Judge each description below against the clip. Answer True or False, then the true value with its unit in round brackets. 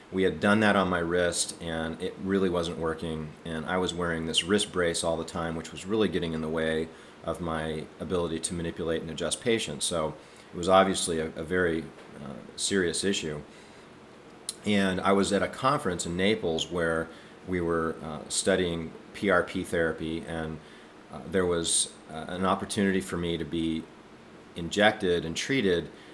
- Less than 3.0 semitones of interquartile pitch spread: True (2.5 semitones)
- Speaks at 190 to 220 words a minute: False (175 wpm)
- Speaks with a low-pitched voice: True (85 Hz)